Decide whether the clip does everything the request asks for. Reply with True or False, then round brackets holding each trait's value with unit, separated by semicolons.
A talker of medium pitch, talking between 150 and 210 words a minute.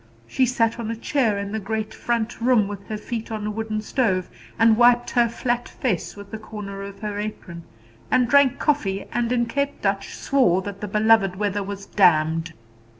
False (215 Hz; 195 wpm)